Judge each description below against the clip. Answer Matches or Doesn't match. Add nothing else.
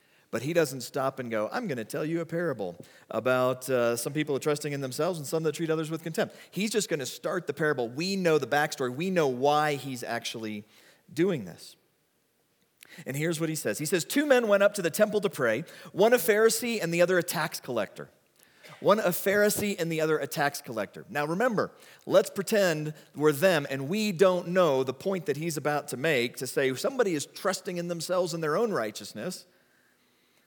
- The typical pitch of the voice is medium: Matches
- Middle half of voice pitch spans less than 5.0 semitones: Doesn't match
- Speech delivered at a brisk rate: Matches